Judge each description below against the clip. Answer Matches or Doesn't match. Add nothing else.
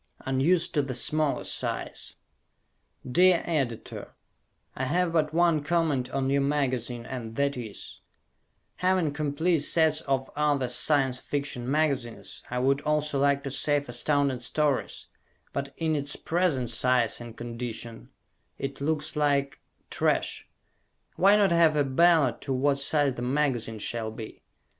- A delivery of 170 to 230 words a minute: Doesn't match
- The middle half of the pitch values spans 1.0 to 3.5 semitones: Matches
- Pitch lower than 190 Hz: Matches